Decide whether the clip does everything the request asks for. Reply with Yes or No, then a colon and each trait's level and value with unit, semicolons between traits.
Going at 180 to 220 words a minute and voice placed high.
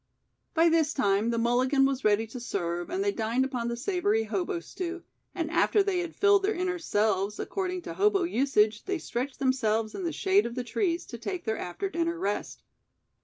Yes: average, 200 wpm; very high, 270 Hz